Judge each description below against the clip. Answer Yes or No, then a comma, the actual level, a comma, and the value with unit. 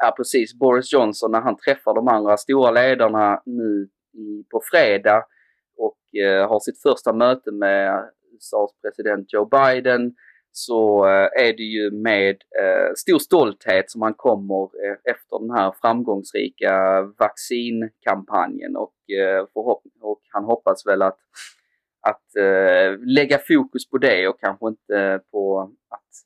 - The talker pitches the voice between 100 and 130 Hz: Yes, low, 105 Hz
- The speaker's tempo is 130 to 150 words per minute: Yes, average, 135 wpm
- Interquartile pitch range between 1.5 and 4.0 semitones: Yes, average, 3.1 semitones